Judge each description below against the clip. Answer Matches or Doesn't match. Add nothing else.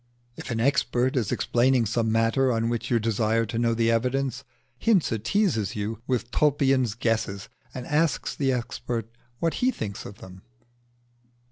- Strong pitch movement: Doesn't match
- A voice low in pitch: Matches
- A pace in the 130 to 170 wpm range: Matches